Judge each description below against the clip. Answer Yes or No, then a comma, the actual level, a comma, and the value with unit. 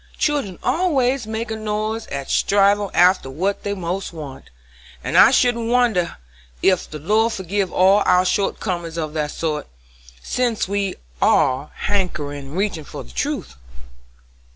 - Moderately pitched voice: No, high, 195 Hz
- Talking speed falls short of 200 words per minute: Yes, average, 150 wpm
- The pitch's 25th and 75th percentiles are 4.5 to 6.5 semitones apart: Yes, average, 5.1 semitones